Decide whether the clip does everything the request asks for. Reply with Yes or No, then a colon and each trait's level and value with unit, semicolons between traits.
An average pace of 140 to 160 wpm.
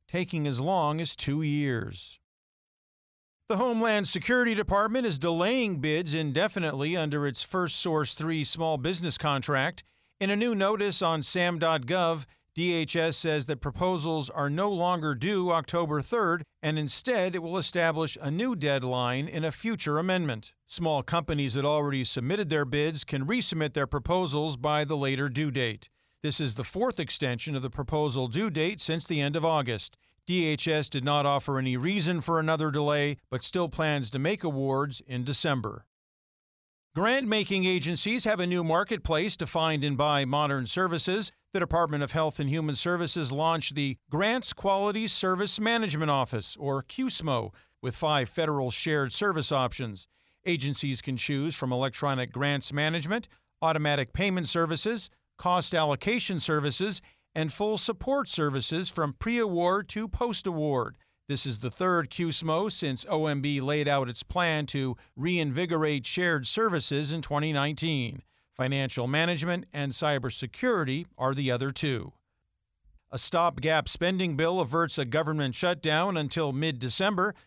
Yes: average, 150 wpm